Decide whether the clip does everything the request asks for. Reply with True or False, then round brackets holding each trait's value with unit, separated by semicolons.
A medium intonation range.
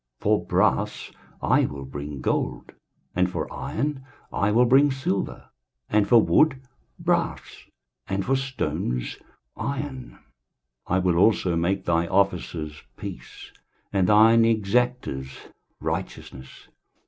False (6.8 semitones)